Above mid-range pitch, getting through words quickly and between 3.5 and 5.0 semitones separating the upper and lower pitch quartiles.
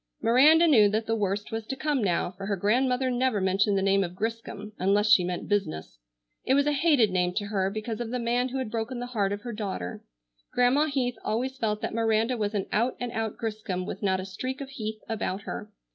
Yes: high, 220 Hz; fast, 230 wpm; average, 3.8 semitones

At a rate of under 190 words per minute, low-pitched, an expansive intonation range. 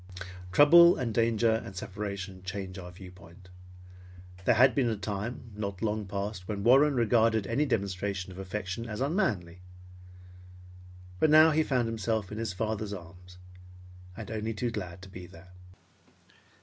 No: average, 150 wpm; low, 105 Hz; average, 3.7 semitones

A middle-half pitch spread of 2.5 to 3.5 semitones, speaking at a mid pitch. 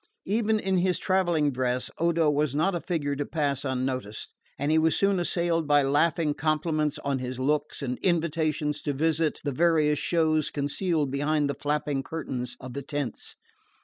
Yes: average, 2.9 semitones; medium, 150 Hz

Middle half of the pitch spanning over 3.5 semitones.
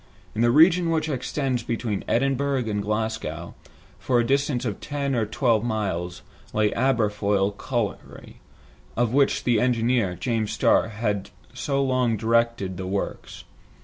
Yes: average, 3.9 semitones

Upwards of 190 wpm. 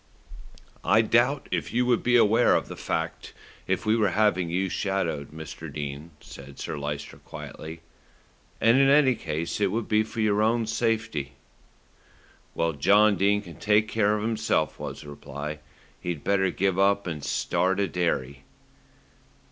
No: average, 160 wpm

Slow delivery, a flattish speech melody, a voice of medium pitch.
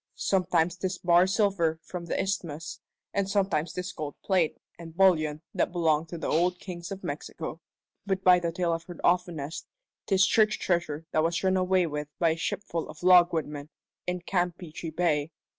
No: average, 175 wpm; narrow, 2.2 semitones; medium, 175 Hz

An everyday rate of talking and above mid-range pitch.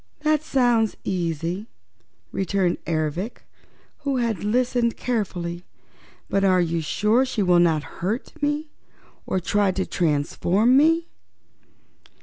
No: slow, 115 wpm; high, 200 Hz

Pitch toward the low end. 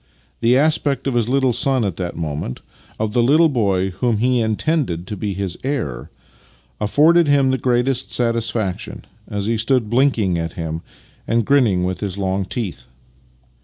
Yes: low, 115 Hz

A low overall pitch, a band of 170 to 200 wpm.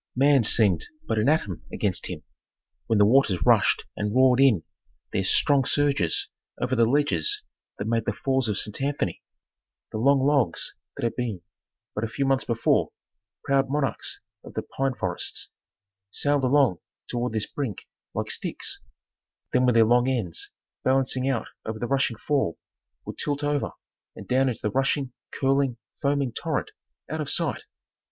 No: low, 130 Hz; average, 160 wpm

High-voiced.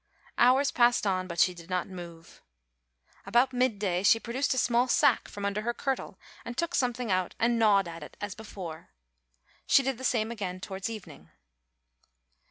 Yes: high, 215 Hz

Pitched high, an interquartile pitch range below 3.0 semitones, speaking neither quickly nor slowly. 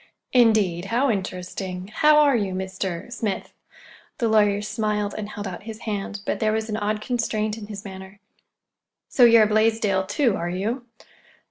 Yes: high, 210 Hz; narrow, 2.6 semitones; average, 160 wpm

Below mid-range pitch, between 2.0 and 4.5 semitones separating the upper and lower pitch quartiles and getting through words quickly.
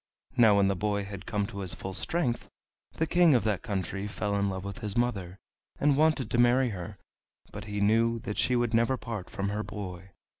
Yes: low, 105 Hz; average, 3.4 semitones; fast, 215 wpm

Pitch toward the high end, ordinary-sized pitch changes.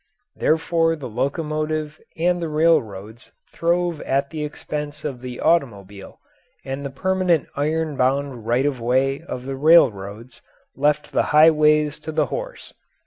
No: medium, 150 Hz; average, 3.7 semitones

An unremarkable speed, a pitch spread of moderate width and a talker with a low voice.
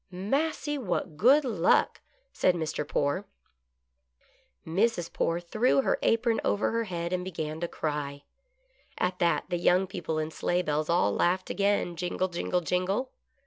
No: average, 155 wpm; average, 3.8 semitones; medium, 180 Hz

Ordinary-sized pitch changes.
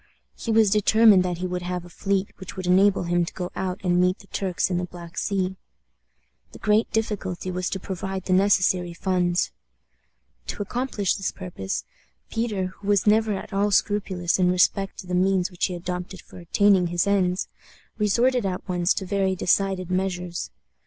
No: narrow, 1.9 semitones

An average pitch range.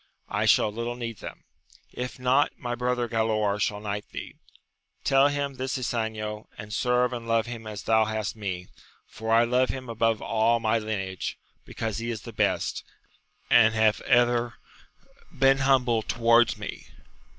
No: narrow, 2.2 semitones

